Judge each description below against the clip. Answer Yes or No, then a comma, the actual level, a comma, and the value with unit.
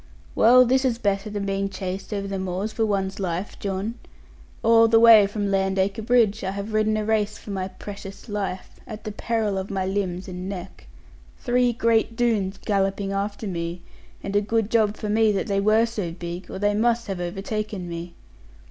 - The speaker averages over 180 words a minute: Yes, average, 190 wpm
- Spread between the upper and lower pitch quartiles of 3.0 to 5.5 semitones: No, narrow, 2.4 semitones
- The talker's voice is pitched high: Yes, high, 200 Hz